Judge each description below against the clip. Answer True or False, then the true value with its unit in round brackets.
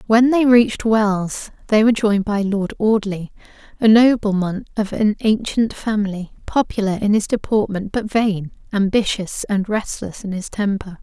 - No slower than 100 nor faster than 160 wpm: True (150 wpm)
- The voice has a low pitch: False (210 Hz)